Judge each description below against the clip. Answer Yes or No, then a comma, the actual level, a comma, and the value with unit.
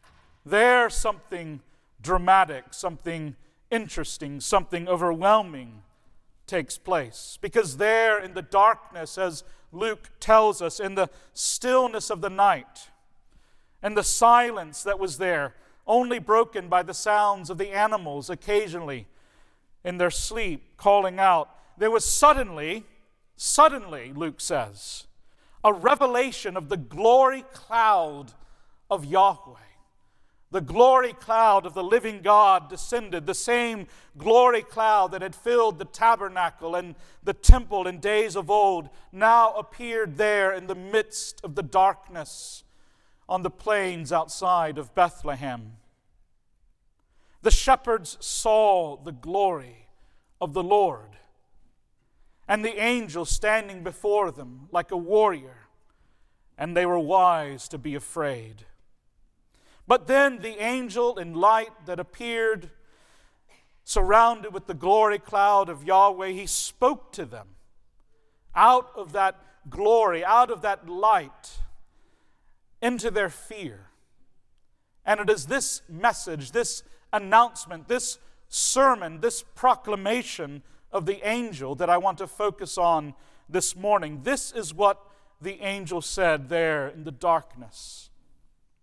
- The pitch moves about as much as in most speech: Yes, average, 4.9 semitones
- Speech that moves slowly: Yes, slow, 125 wpm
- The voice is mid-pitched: No, high, 195 Hz